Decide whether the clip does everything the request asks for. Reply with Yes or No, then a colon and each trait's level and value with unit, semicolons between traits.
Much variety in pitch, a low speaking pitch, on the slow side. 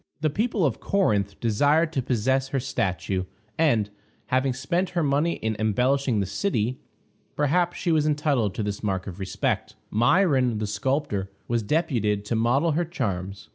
No: wide, 6.4 semitones; low, 130 Hz; average, 160 wpm